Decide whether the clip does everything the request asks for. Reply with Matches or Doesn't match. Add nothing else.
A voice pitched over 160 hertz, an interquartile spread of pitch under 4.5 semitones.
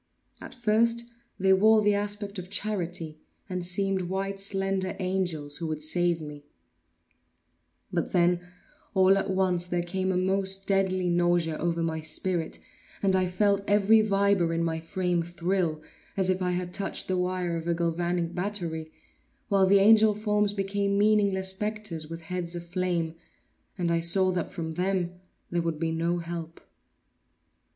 Matches